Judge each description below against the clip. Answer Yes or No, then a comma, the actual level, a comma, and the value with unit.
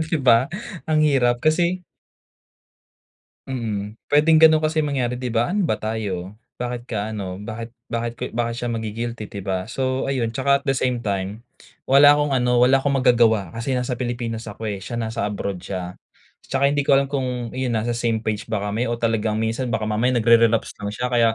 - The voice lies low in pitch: Yes, low, 120 Hz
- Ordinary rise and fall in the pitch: Yes, average, 3.3 semitones